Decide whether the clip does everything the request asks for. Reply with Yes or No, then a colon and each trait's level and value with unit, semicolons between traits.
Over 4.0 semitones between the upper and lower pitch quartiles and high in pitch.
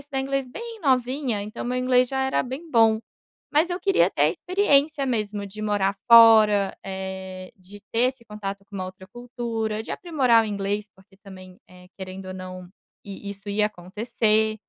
Yes: average, 4.4 semitones; high, 215 Hz